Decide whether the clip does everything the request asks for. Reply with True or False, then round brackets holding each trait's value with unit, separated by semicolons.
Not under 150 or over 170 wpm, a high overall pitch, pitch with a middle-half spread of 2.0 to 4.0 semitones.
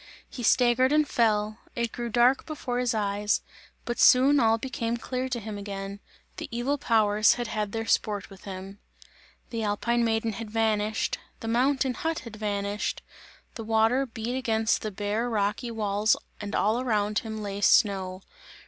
True (165 wpm; 225 Hz; 2.6 semitones)